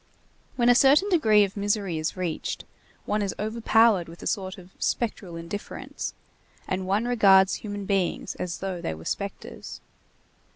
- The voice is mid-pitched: No, high, 200 Hz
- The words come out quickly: No, average, 155 wpm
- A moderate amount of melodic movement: Yes, average, 3.0 semitones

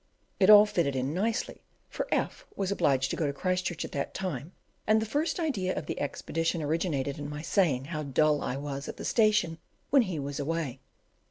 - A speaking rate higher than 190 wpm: Yes, average, 200 wpm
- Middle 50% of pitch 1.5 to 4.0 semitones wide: No, wide, 5.6 semitones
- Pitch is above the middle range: No, medium, 165 Hz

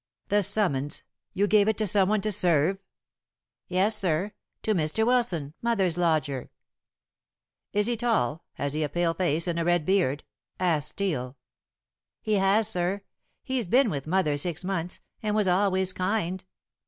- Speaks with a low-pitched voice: No, medium, 185 Hz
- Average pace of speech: Yes, average, 155 wpm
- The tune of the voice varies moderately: Yes, average, 4.4 semitones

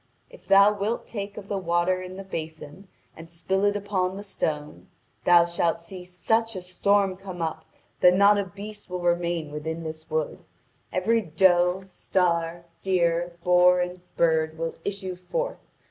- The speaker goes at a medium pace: Yes, average, 160 wpm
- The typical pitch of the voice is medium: Yes, medium, 180 Hz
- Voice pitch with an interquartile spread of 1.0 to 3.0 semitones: Yes, average, 2.7 semitones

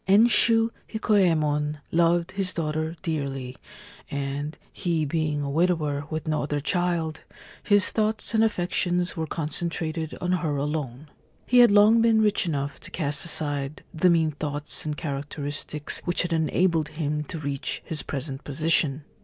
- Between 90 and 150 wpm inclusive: Yes, average, 145 wpm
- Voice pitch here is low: No, medium, 160 Hz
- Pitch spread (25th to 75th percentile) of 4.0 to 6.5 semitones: No, average, 3.4 semitones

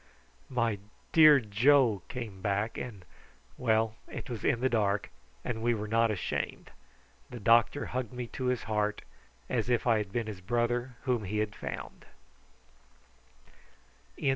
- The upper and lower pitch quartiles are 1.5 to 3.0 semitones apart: Yes, average, 2.7 semitones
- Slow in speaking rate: No, average, 145 wpm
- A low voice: Yes, low, 115 Hz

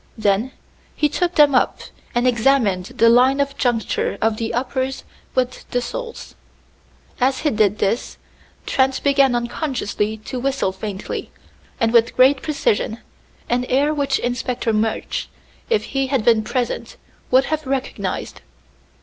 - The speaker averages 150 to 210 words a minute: No, average, 140 wpm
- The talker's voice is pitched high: Yes, very high, 250 Hz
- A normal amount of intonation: Yes, average, 3.2 semitones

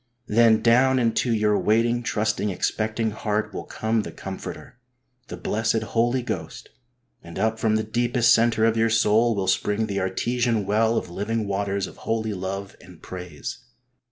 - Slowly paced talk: No, average, 160 wpm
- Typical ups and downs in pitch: No, narrow, 2.1 semitones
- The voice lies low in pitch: Yes, low, 110 Hz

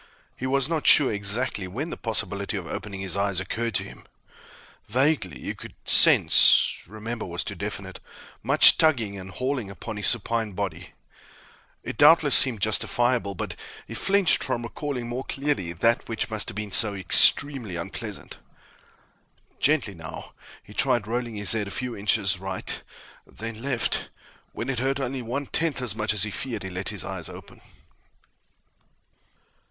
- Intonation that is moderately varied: Yes, average, 4.4 semitones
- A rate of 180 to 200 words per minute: No, average, 160 wpm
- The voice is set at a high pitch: No, low, 110 Hz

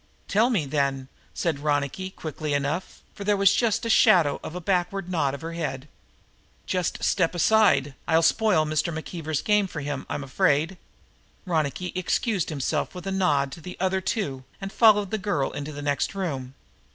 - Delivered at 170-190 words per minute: Yes, average, 175 wpm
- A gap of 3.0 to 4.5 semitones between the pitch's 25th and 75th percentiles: No, average, 4.9 semitones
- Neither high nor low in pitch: Yes, medium, 165 Hz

